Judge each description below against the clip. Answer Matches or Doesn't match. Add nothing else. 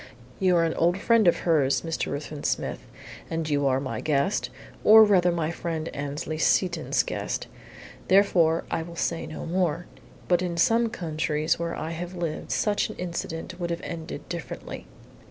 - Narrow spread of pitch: Matches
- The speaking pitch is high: Doesn't match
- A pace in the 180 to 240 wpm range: Doesn't match